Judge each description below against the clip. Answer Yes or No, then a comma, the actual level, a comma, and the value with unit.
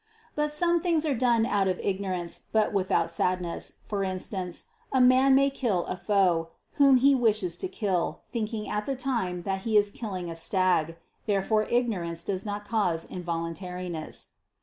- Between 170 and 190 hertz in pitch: No, high, 200 Hz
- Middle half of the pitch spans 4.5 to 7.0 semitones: Yes, average, 5.1 semitones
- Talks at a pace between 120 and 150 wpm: No, average, 165 wpm